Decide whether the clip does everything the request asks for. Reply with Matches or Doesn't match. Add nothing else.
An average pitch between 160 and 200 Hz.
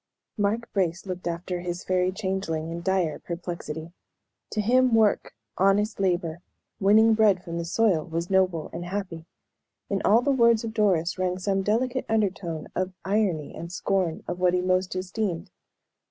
Matches